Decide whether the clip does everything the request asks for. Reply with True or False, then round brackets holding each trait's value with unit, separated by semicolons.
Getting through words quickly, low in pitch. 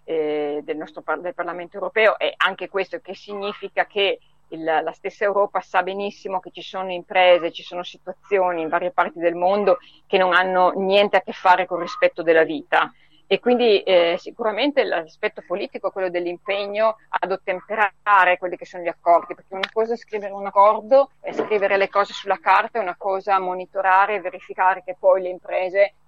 False (190 wpm; 190 Hz)